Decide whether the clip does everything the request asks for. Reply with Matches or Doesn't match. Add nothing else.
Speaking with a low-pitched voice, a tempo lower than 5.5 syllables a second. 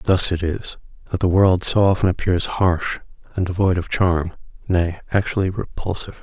Matches